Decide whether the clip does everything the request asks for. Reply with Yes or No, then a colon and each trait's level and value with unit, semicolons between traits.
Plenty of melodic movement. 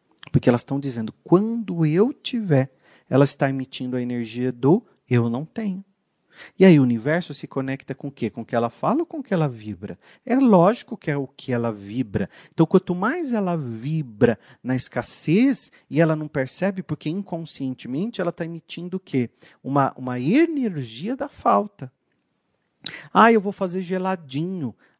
Yes: wide, 6.6 semitones